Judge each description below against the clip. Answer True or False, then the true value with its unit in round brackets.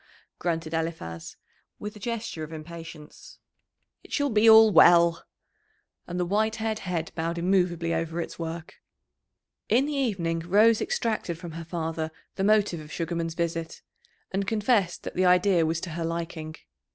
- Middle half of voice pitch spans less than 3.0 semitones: False (4.1 semitones)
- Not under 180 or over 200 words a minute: False (155 wpm)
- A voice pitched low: False (170 Hz)